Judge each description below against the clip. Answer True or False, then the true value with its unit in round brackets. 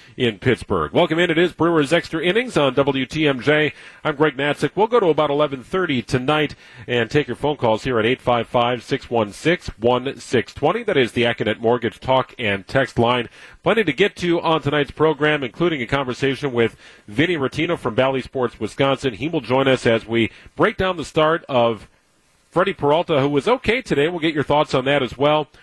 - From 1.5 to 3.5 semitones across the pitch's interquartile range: False (4.1 semitones)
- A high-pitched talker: False (140 Hz)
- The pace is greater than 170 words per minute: True (205 wpm)